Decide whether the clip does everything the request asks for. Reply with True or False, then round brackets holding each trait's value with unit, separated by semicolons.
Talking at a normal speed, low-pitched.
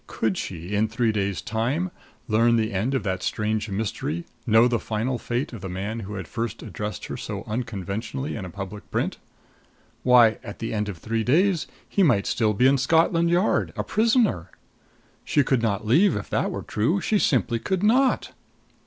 True (190 wpm; 115 Hz)